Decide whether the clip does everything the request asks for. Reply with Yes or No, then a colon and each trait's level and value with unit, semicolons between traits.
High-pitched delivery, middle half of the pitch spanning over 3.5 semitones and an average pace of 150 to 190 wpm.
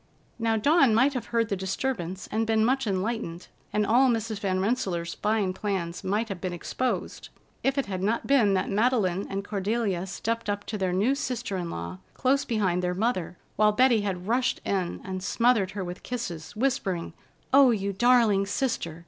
Yes: high, 210 Hz; average, 4.1 semitones; average, 180 wpm